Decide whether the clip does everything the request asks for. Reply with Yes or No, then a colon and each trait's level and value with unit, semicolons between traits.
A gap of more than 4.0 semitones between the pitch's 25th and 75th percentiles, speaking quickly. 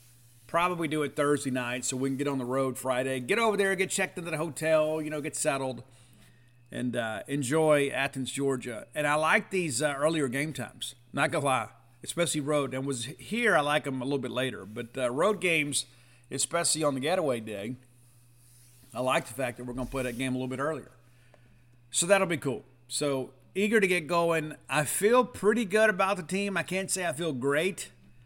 Yes: average, 4.5 semitones; fast, 210 wpm